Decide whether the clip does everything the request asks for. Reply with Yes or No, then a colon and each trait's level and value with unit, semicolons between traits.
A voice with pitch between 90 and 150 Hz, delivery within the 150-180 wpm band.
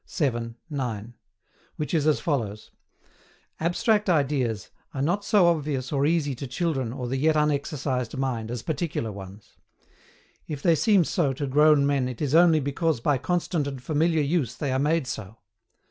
Yes: medium, 140 Hz; average, 165 wpm